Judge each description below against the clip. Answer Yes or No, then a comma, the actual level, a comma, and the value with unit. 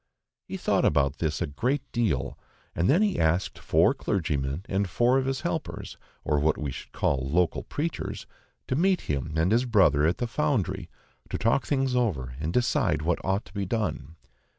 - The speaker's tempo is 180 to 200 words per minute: Yes, average, 185 wpm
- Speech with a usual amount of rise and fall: No, wide, 8.3 semitones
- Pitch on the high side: No, very low, 95 Hz